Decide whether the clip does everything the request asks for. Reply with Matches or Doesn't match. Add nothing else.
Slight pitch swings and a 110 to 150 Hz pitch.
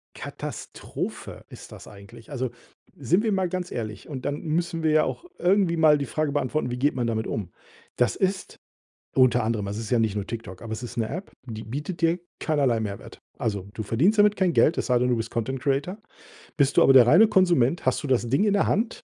Doesn't match